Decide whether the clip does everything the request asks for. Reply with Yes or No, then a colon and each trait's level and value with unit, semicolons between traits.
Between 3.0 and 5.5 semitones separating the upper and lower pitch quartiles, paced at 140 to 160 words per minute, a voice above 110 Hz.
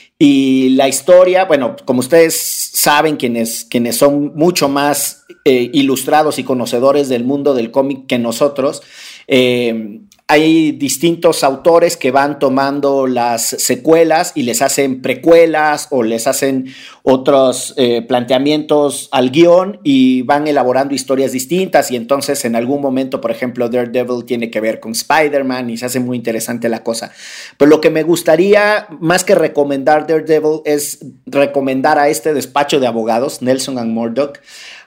Yes: average, 3.4 semitones; average, 150 wpm; medium, 140 Hz